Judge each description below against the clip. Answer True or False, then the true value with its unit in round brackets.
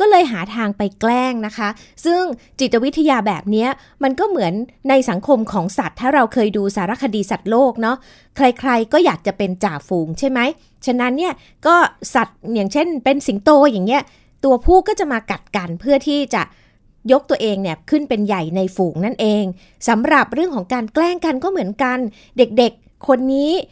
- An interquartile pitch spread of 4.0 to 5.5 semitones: True (5.1 semitones)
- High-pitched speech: True (245 Hz)